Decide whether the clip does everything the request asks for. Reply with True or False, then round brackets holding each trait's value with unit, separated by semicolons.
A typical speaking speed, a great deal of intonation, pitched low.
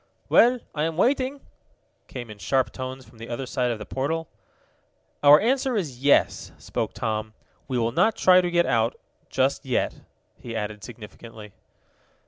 True (160 wpm; 7.0 semitones; 130 Hz)